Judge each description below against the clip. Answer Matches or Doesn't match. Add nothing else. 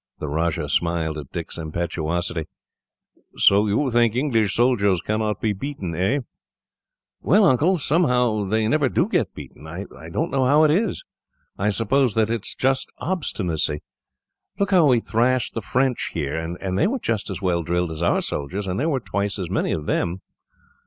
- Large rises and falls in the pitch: Matches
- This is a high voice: Doesn't match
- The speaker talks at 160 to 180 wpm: Matches